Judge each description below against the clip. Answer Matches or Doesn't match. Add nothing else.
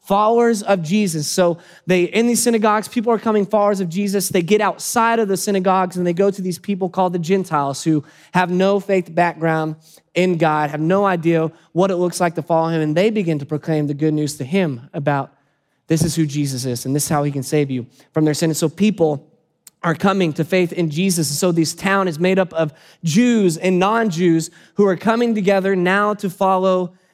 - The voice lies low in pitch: Doesn't match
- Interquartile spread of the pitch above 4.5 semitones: Doesn't match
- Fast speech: Matches